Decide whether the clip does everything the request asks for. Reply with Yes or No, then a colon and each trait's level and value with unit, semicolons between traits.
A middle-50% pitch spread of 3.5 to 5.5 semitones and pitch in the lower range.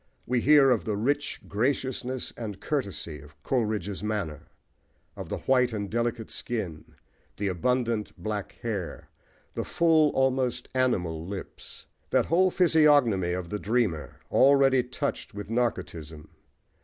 Yes: average, 5.0 semitones; low, 115 Hz